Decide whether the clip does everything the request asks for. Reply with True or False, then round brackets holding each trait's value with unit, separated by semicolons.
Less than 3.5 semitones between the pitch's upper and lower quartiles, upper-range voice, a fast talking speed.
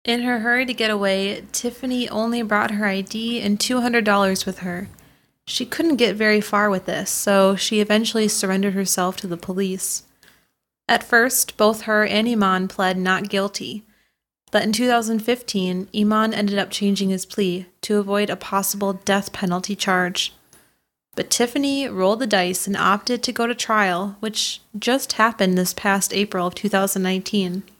False (2.6 semitones; 205 Hz; 160 wpm)